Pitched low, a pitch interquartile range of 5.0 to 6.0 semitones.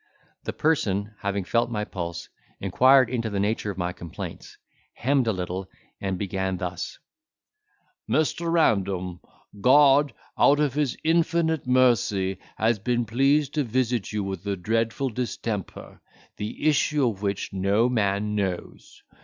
Yes: low, 110 Hz; average, 5.3 semitones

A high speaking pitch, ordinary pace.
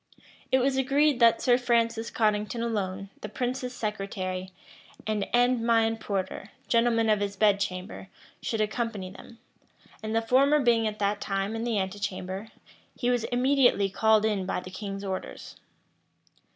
Yes: high, 220 Hz; average, 150 wpm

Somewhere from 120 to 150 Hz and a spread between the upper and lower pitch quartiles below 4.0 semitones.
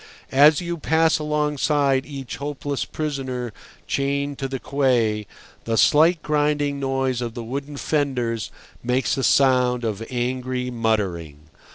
Yes: low, 135 Hz; average, 3.0 semitones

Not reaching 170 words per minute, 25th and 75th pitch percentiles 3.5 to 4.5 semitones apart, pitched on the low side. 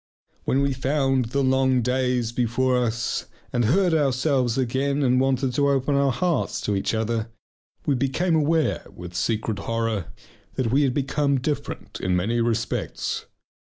No: average, 155 wpm; average, 3.1 semitones; low, 130 Hz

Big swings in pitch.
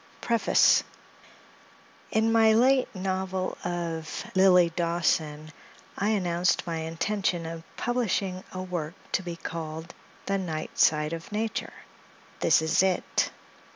No: average, 3.0 semitones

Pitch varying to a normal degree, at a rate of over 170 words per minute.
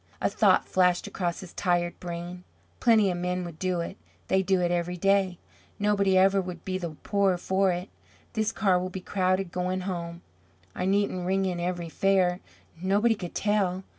No: narrow, 1.6 semitones; average, 180 wpm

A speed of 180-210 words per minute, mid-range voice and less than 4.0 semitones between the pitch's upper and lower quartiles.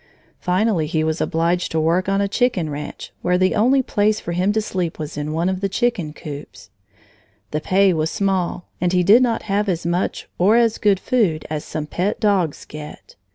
No: average, 200 wpm; medium, 180 Hz; average, 4.3 semitones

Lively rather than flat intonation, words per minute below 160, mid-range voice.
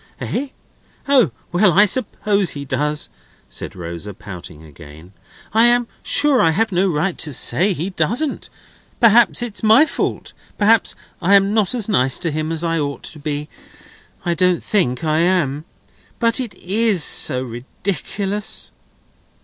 Yes: wide, 6.7 semitones; average, 150 wpm; medium, 180 Hz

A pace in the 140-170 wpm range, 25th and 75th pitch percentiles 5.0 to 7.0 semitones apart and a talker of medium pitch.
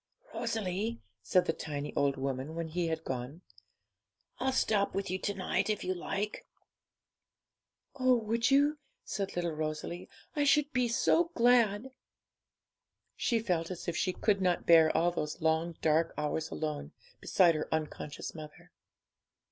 Yes: average, 150 wpm; wide, 5.5 semitones; medium, 175 Hz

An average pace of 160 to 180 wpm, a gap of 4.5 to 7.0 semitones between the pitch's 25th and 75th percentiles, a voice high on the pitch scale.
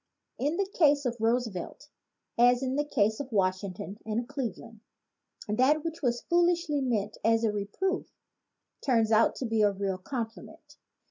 No: average, 150 wpm; average, 5.1 semitones; high, 235 Hz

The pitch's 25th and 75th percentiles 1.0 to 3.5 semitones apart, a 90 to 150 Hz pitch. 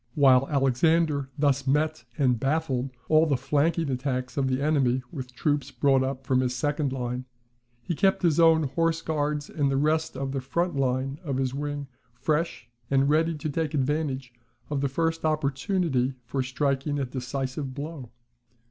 Yes: average, 2.8 semitones; medium, 140 Hz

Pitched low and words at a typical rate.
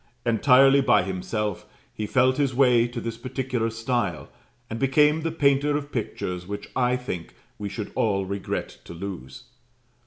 Yes: low, 120 Hz; average, 155 wpm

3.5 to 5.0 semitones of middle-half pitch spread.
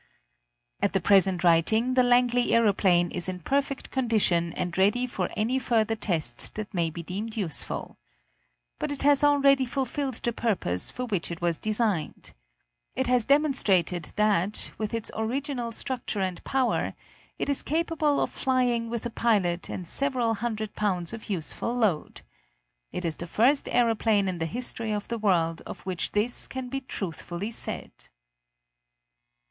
No: wide, 5.4 semitones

